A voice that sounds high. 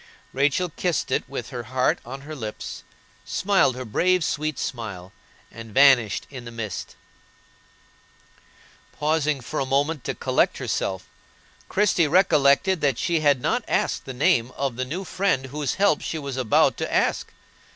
No: medium, 140 Hz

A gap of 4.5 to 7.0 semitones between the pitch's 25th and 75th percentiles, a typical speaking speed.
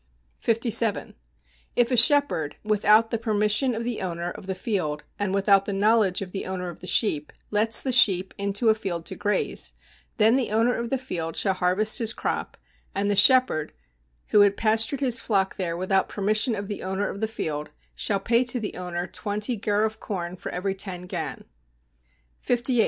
No: average, 3.3 semitones; average, 190 wpm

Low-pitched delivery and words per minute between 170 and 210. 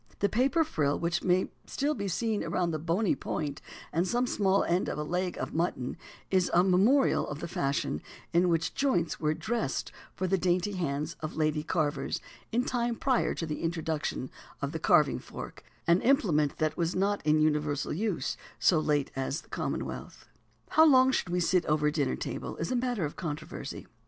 No: medium, 170 Hz; average, 185 wpm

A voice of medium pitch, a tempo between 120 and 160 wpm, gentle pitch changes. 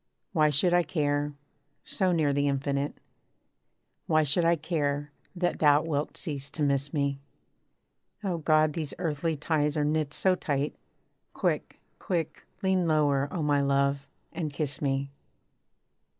Yes: medium, 150 Hz; average, 140 wpm; narrow, 2.3 semitones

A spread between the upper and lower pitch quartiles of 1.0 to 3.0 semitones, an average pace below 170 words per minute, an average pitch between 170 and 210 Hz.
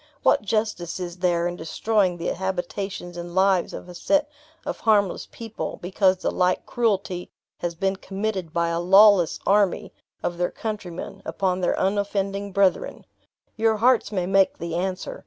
Yes: narrow, 2.6 semitones; average, 155 wpm; high, 190 Hz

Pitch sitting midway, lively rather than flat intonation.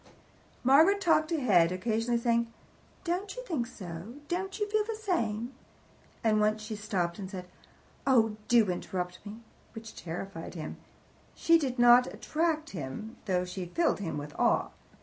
No: high, 225 Hz; wide, 8.8 semitones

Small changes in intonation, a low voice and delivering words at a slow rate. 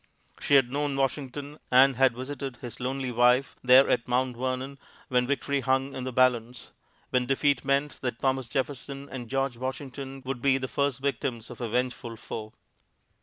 No: narrow, 1.7 semitones; low, 130 Hz; average, 170 wpm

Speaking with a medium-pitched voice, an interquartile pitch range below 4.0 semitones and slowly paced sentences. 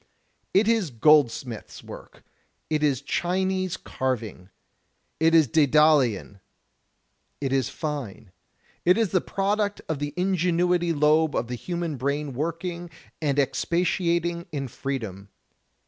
No: medium, 155 Hz; average, 4.6 semitones; slow, 115 wpm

